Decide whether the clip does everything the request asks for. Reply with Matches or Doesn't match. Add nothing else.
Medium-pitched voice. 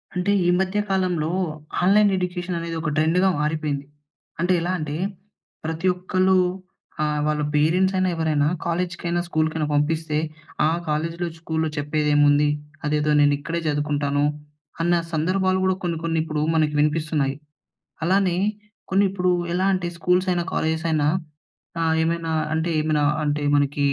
Matches